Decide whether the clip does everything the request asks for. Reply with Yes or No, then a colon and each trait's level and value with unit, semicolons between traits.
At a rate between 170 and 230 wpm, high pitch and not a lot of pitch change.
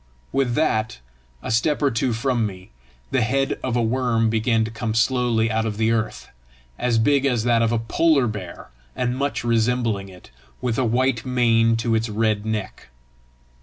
No: average, 180 wpm; low, 115 Hz; narrow, 2.1 semitones